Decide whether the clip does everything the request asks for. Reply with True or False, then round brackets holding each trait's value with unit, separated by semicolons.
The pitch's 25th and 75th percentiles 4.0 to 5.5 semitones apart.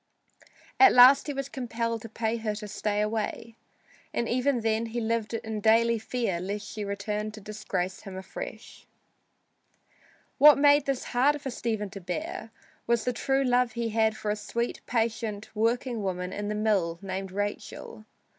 False (2.5 semitones)